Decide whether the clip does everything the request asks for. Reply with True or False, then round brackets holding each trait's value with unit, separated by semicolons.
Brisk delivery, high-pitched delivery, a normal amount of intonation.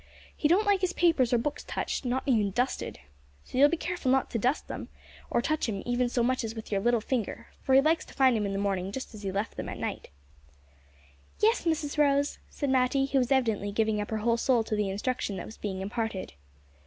True (240 wpm; 245 Hz; 4.6 semitones)